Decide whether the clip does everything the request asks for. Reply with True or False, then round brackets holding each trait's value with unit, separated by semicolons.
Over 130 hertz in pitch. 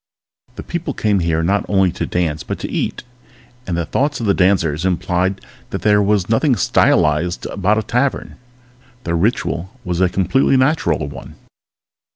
False (95 Hz)